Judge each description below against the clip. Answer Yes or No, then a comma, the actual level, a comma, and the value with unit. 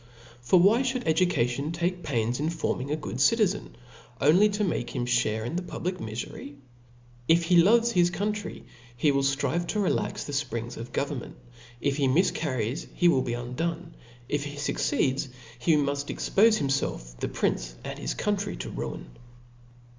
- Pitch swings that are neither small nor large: No, wide, 5.9 semitones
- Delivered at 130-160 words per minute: No, average, 175 wpm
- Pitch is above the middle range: No, medium, 150 Hz